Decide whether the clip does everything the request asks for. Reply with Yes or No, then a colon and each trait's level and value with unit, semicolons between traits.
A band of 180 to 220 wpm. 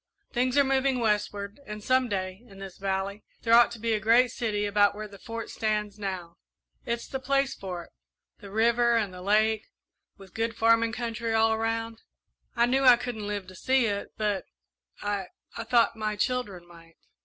Yes: average, 190 wpm